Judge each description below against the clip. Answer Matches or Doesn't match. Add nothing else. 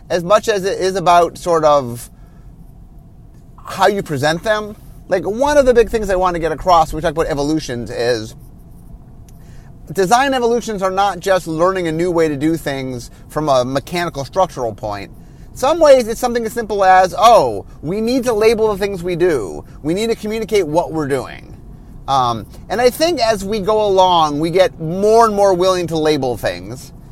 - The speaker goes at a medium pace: Matches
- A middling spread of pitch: Doesn't match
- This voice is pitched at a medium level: Matches